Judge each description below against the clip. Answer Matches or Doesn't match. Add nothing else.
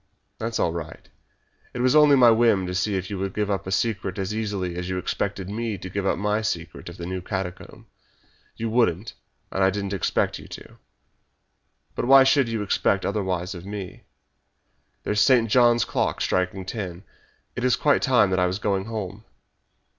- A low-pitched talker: Matches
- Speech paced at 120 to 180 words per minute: Doesn't match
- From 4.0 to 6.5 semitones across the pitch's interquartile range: Doesn't match